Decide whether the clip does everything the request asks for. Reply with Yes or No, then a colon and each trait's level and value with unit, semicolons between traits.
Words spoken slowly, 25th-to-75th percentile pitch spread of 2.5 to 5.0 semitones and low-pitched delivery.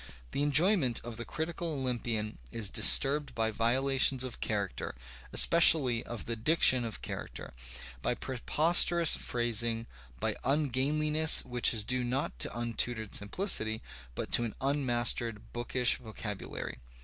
Yes: slow, 125 wpm; average, 3.9 semitones; low, 120 Hz